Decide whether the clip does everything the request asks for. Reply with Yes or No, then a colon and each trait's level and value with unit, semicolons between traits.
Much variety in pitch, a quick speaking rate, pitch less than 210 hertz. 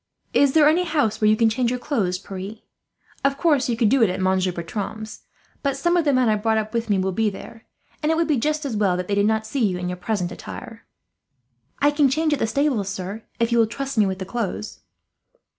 No: wide, 5.7 semitones; fast, 245 wpm; high, 225 Hz